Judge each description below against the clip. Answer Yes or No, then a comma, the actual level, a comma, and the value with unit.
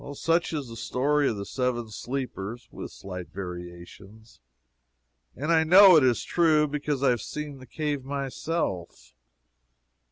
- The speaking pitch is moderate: No, low, 130 Hz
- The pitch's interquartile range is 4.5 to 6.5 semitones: Yes, wide, 5.6 semitones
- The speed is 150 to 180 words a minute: No, average, 140 wpm